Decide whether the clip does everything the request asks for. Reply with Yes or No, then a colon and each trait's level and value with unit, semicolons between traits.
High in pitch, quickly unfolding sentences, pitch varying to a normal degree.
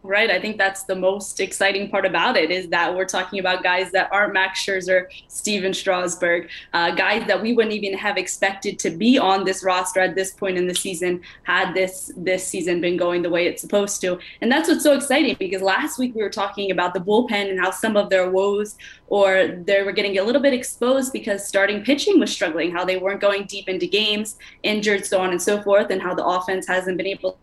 No: high, 195 Hz; fast, 230 wpm; narrow, 1.9 semitones